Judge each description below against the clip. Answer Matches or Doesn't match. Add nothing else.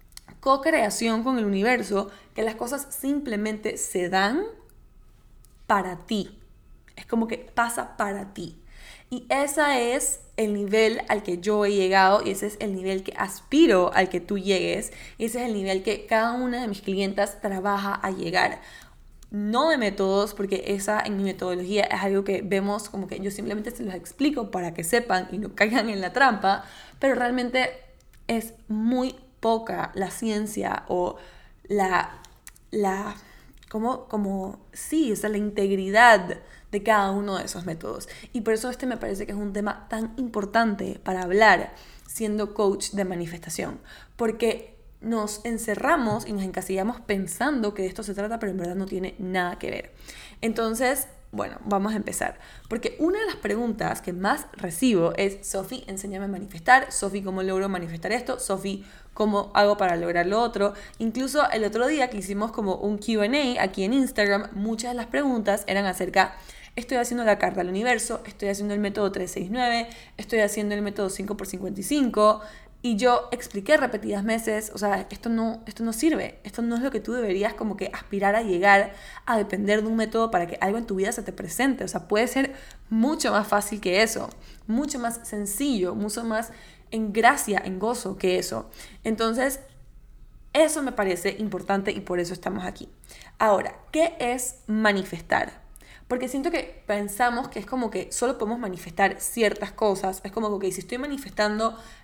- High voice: Matches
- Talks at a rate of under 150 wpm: Doesn't match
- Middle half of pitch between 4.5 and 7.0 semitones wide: Doesn't match